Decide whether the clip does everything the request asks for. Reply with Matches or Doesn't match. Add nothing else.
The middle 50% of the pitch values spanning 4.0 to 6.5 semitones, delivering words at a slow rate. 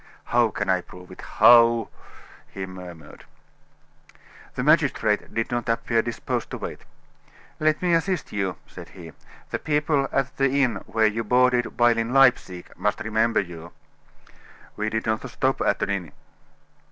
Doesn't match